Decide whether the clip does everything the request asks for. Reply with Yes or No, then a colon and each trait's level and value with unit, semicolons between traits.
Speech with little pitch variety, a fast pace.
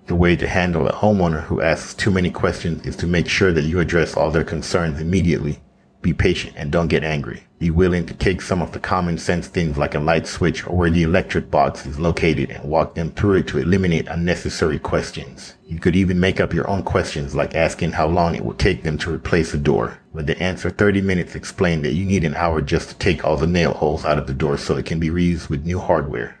Yes: narrow, 2.1 semitones; fast, 245 wpm